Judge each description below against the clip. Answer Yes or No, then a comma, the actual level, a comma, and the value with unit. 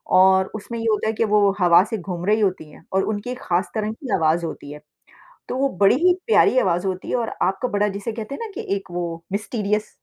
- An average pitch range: Yes, average, 3.4 semitones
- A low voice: No, high, 200 Hz